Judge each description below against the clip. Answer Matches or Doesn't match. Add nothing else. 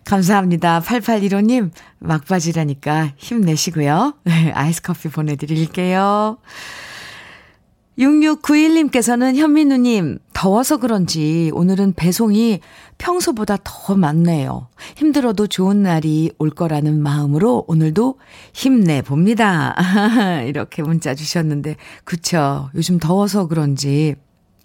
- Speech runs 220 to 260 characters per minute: Matches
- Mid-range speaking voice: Matches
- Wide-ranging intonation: Matches